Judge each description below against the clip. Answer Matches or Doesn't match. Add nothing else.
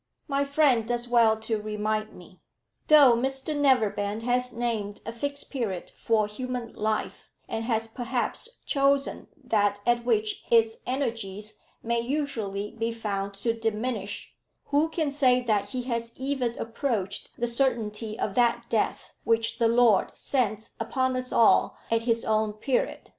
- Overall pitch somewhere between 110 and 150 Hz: Doesn't match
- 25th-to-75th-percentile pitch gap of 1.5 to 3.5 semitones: Matches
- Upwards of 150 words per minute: Doesn't match